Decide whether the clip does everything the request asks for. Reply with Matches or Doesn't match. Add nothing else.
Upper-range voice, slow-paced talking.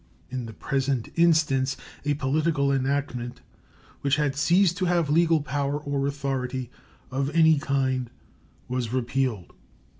Doesn't match